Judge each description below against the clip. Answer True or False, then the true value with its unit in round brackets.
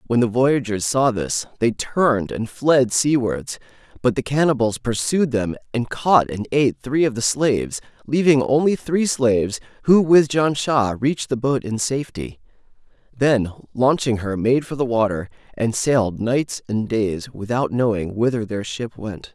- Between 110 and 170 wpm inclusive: True (165 wpm)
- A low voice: True (120 Hz)